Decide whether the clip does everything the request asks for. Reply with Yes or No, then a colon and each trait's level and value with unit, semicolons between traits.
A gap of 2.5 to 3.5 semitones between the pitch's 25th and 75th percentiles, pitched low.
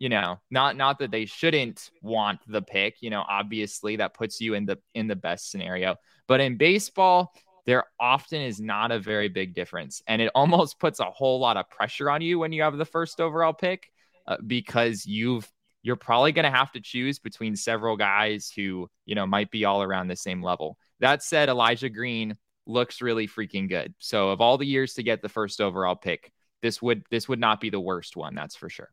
No: average, 4.5 semitones; low, 115 Hz